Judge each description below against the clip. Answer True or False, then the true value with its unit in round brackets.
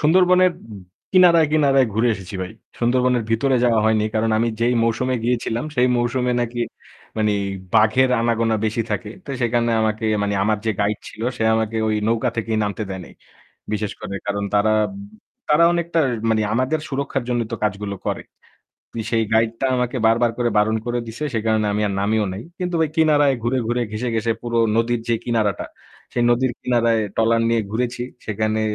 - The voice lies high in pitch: False (115 Hz)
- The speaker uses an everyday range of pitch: False (2.3 semitones)